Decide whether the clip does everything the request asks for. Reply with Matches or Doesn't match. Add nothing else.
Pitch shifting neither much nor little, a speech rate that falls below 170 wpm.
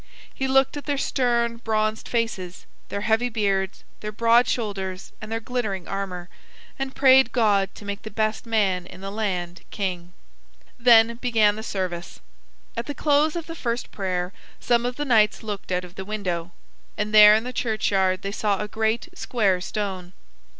Doesn't match